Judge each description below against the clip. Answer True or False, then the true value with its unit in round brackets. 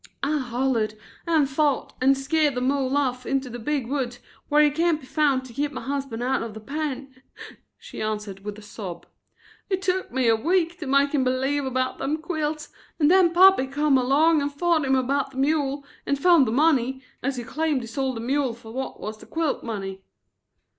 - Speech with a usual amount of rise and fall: True (3.2 semitones)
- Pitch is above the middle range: True (270 Hz)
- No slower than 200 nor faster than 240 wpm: True (205 wpm)